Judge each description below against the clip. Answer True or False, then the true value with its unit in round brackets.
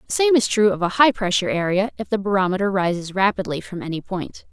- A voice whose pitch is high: True (195 Hz)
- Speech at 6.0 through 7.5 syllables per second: True (6.3 syllables/s)